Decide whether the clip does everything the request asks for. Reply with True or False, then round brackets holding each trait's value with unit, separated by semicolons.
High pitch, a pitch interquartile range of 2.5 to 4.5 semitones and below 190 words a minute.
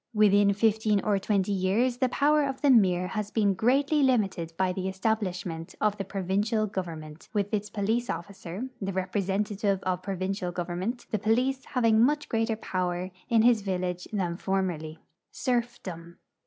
True (200 Hz; 3.4 semitones; 160 wpm)